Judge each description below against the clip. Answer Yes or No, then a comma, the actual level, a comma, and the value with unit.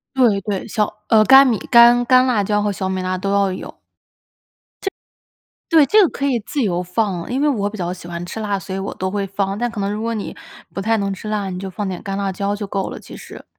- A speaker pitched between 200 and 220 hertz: Yes, high, 205 Hz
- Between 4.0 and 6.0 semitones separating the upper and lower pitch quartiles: No, average, 3.1 semitones